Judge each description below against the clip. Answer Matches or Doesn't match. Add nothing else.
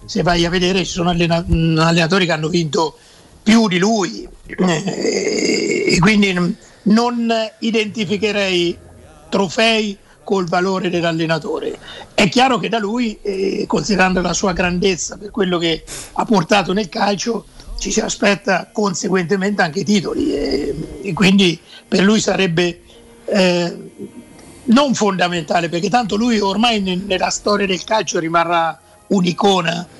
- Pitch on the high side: Matches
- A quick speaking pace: Doesn't match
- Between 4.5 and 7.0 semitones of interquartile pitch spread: Doesn't match